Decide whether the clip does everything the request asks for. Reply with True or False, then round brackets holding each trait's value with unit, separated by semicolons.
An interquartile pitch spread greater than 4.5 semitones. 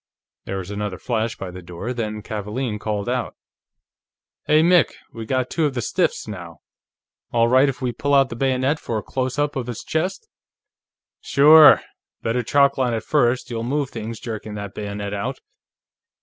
False (4.2 semitones)